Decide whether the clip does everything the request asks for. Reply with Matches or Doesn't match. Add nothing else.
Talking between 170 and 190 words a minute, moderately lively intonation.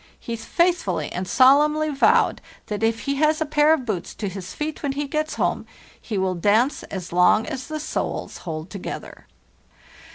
Doesn't match